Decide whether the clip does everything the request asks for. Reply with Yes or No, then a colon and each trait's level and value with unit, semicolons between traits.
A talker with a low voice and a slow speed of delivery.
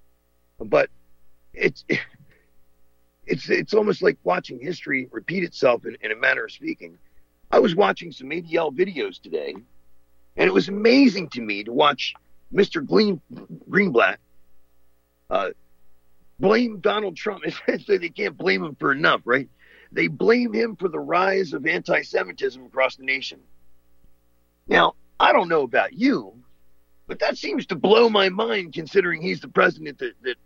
No: low, 115 Hz; average, 150 wpm